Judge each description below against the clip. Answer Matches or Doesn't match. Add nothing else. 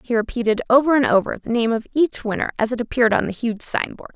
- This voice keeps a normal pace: Doesn't match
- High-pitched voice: Matches